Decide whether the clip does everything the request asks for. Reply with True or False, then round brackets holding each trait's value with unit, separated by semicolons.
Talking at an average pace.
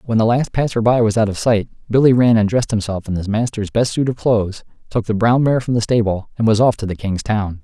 False (275 wpm)